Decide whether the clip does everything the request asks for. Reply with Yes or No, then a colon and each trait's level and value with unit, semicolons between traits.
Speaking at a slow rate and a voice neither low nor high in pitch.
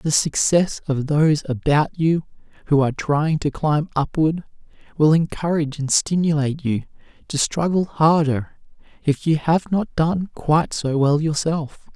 No: average, 145 wpm; medium, 150 Hz